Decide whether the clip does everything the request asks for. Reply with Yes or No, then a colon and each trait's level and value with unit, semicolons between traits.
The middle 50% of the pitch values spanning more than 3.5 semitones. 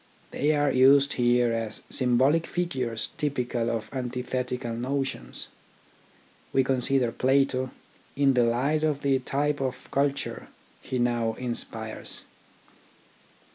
No: narrow, 2.5 semitones